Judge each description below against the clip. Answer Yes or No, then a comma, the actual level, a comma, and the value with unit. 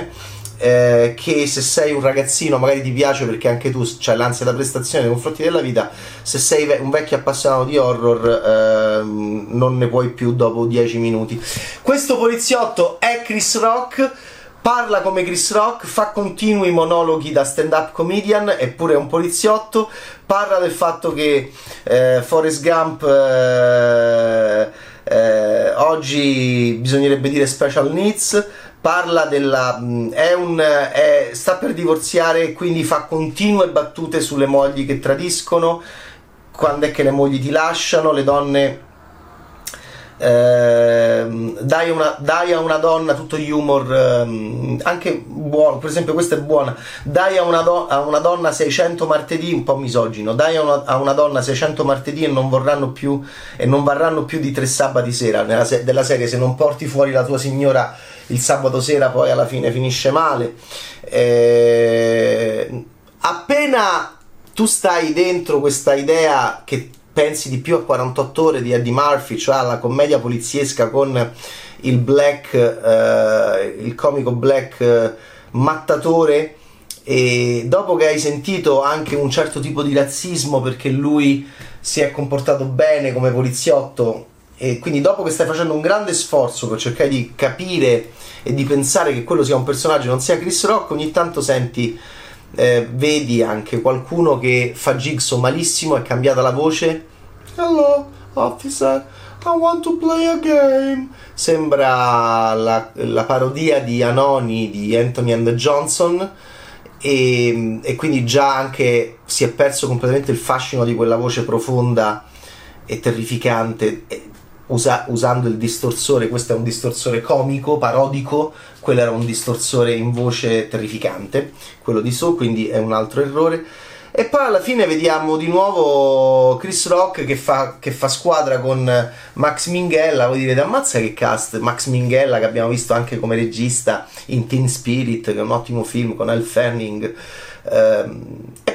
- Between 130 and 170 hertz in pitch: Yes, low, 135 Hz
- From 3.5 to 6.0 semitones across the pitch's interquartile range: Yes, average, 5.0 semitones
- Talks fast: No, average, 150 wpm